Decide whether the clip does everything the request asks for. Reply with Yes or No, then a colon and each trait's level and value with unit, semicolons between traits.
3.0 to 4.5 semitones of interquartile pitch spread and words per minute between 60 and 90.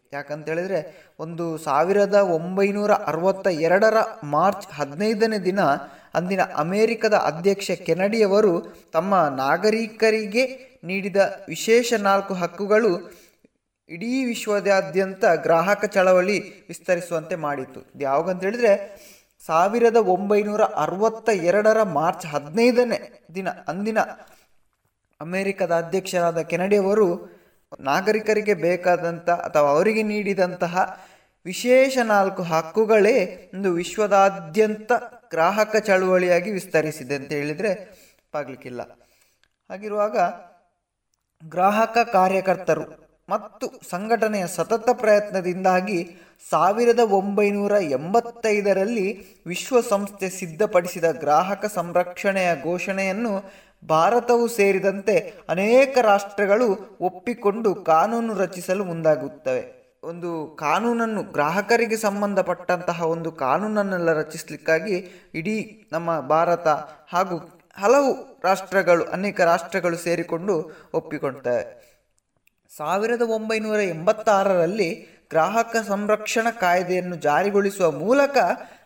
Yes: average, 4.0 semitones; average, 80 wpm